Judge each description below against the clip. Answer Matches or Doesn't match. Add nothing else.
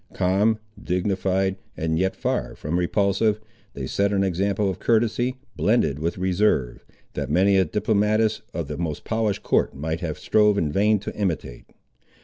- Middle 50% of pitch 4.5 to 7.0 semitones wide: Doesn't match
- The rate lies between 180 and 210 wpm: Doesn't match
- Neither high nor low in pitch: Doesn't match